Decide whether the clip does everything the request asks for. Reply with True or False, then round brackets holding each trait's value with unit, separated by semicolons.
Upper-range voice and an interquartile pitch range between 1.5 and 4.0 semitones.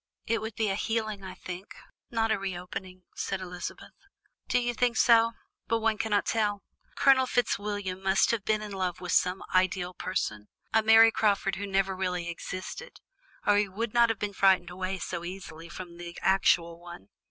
True (195 Hz; 3.3 semitones)